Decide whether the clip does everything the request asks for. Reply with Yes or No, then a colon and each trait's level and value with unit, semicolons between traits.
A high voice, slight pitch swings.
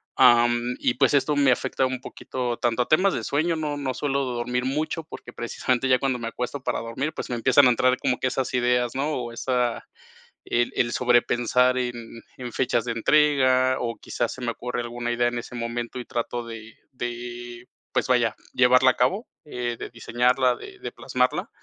No: low, 125 Hz; narrow, 1.5 semitones